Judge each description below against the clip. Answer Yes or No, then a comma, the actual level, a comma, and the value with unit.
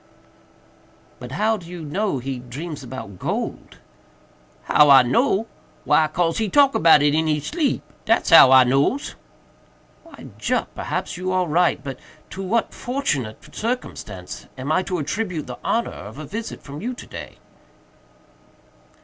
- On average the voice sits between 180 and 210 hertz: No, medium, 160 Hz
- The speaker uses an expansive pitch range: Yes, wide, 7.7 semitones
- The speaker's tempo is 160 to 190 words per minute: No, average, 150 wpm